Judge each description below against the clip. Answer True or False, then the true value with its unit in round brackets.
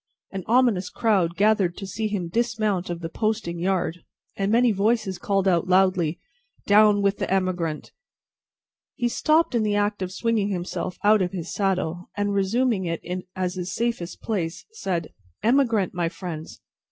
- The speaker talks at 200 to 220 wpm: False (160 wpm)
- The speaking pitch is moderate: False (195 Hz)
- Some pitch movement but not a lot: True (3.4 semitones)